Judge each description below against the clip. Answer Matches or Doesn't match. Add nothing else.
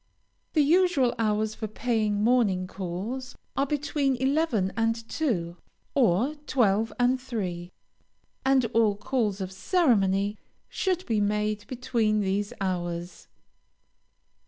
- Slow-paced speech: Matches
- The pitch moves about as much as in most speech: Matches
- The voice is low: Doesn't match